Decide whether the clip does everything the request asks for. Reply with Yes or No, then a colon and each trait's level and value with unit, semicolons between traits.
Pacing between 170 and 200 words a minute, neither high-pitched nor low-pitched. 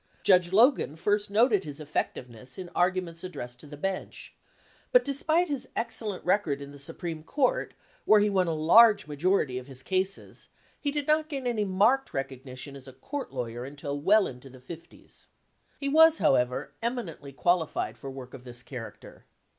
Yes: average, 175 wpm; medium, 175 Hz